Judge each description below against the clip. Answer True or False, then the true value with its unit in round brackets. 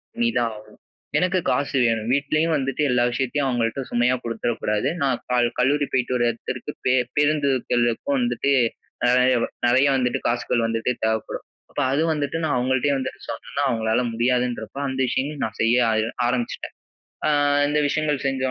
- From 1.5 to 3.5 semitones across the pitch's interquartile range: True (3.2 semitones)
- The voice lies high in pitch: False (125 Hz)